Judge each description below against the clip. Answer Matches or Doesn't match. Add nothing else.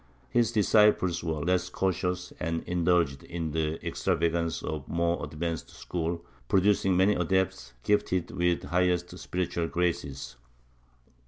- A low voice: Matches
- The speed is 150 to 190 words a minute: Doesn't match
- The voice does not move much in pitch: Matches